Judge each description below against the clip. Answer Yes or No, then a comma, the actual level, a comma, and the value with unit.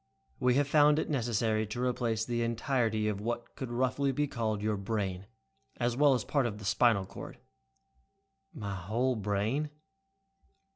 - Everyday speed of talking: Yes, average, 155 wpm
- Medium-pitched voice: No, low, 115 Hz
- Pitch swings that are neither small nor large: Yes, average, 3.3 semitones